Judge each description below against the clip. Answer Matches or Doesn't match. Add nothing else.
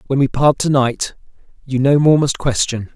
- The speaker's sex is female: Doesn't match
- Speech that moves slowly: Doesn't match